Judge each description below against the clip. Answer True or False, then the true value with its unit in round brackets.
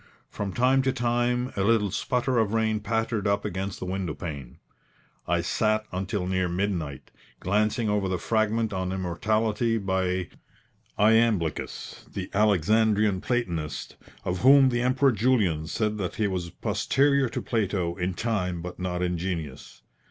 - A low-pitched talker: True (100 Hz)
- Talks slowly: False (145 wpm)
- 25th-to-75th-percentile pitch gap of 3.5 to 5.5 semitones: True (3.9 semitones)